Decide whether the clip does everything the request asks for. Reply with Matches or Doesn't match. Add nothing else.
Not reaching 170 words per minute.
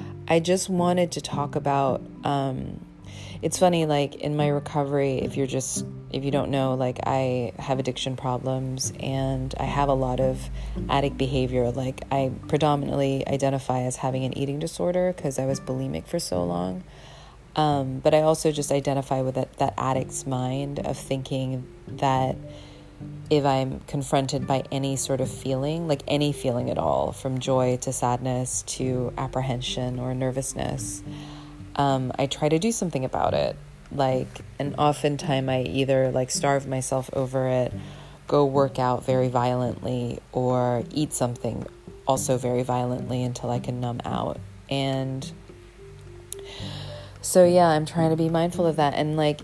Matches